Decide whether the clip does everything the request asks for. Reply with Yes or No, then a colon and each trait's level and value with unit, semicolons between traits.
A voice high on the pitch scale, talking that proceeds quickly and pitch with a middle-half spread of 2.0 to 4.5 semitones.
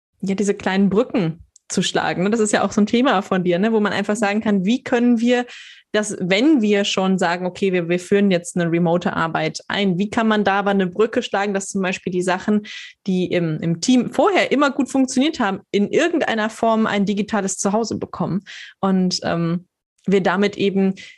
Yes: high, 200 Hz; fast, 205 wpm; average, 2.9 semitones